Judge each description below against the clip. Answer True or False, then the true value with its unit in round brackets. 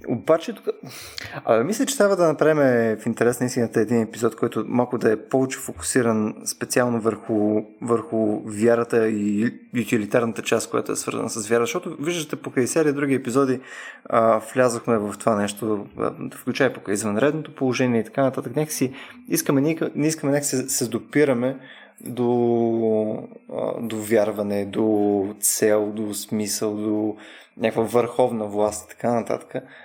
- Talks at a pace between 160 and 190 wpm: False (145 wpm)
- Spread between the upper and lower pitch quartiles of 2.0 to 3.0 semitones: False (3.6 semitones)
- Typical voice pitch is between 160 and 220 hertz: False (115 Hz)